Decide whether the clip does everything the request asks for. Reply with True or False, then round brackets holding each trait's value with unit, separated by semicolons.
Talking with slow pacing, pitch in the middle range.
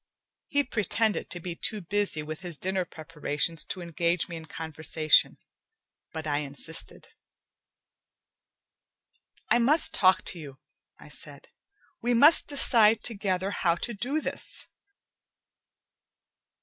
True (120 wpm; 180 Hz)